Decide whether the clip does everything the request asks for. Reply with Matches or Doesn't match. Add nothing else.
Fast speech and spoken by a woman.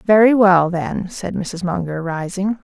Doesn't match